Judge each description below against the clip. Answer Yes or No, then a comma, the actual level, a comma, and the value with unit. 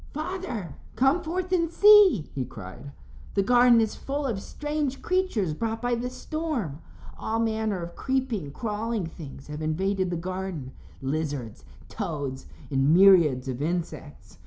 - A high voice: Yes, high, 200 Hz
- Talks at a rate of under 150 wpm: Yes, average, 140 wpm